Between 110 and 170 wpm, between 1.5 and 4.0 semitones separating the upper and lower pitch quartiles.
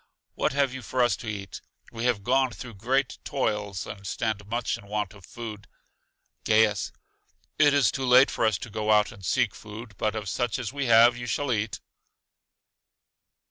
No: average, 185 wpm; average, 3.2 semitones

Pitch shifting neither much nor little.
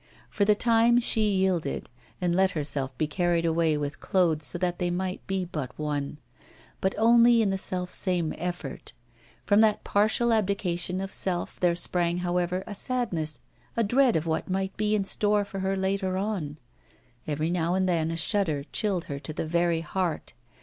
Yes: average, 3.4 semitones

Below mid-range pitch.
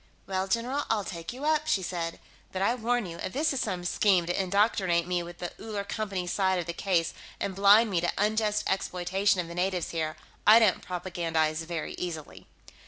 No: high, 190 Hz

